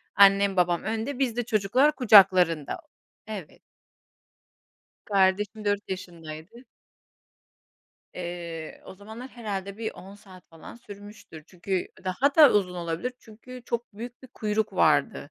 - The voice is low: No, high, 200 Hz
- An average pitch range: Yes, average, 3.7 semitones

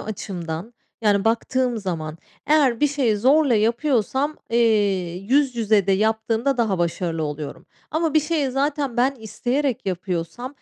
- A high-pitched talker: Yes, high, 230 Hz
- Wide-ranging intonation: Yes, wide, 5.7 semitones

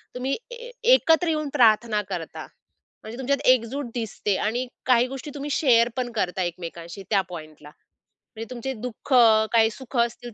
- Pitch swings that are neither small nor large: Yes, average, 4.0 semitones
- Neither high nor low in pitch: No, high, 235 Hz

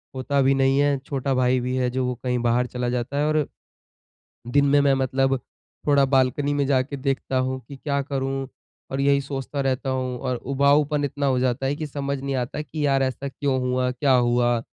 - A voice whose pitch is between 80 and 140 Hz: Yes, low, 135 Hz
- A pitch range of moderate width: No, narrow, 1.7 semitones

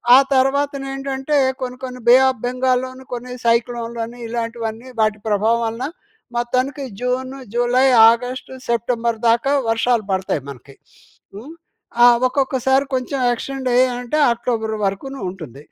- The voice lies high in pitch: Yes, high, 245 Hz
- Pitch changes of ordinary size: No, narrow, 2.3 semitones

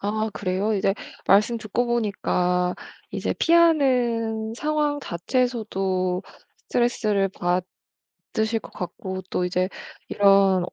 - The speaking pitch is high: Yes, high, 210 Hz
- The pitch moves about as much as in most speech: Yes, average, 4.3 semitones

